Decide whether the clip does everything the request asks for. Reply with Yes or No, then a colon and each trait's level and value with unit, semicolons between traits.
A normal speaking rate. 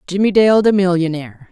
Yes: average, 160 wpm